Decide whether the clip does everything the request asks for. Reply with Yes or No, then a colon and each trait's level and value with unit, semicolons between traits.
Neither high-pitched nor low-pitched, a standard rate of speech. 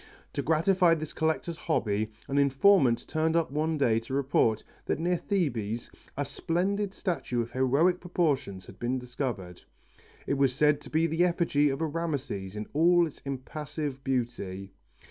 Yes: medium, 145 Hz; average, 160 wpm